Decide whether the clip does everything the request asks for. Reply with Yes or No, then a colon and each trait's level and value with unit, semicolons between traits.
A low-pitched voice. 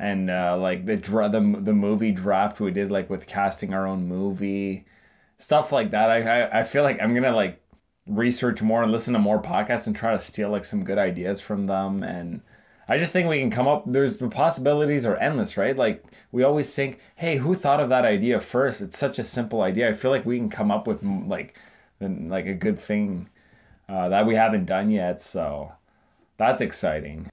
Yes: low, 110 Hz